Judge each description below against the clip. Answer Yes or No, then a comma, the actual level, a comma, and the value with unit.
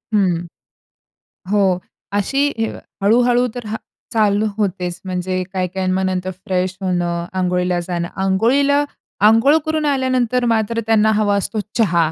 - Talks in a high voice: Yes, high, 200 Hz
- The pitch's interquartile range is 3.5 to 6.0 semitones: Yes, average, 4.4 semitones